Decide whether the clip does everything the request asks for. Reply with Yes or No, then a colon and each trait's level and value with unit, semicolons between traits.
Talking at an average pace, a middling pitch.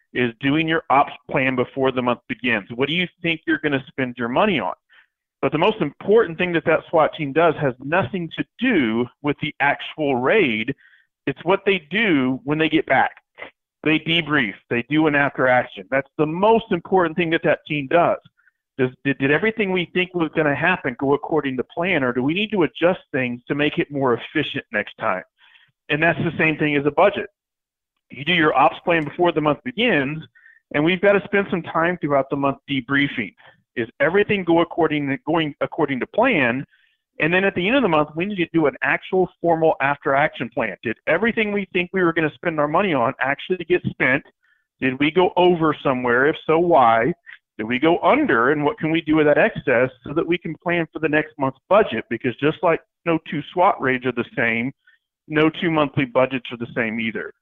No: fast, 215 wpm; medium, 155 Hz